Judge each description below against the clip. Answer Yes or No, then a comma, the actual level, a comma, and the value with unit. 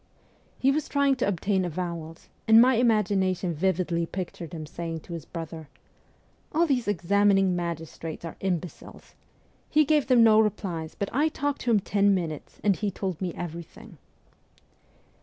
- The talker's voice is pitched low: No, high, 190 Hz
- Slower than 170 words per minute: Yes, average, 160 wpm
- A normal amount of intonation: Yes, average, 4.7 semitones